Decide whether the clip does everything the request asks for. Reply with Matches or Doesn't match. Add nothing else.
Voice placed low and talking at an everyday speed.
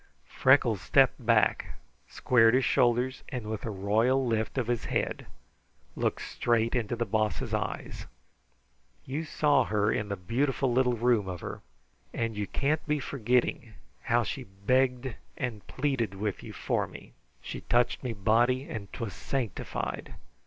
Matches